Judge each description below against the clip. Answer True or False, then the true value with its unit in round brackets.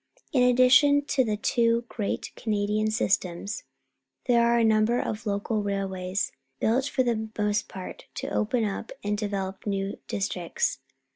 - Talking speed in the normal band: True (145 wpm)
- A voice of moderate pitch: False (215 Hz)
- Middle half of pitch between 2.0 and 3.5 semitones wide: True (2.9 semitones)